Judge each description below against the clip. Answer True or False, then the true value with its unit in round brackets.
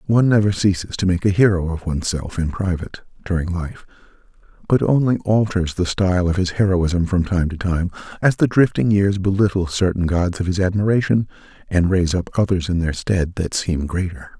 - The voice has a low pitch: True (95 Hz)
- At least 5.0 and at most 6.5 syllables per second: True (5.4 syllables/s)